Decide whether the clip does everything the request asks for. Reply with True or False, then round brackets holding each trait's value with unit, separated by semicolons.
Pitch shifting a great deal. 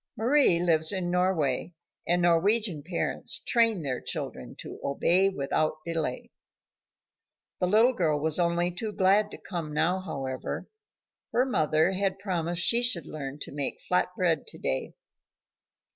False (3.9 semitones)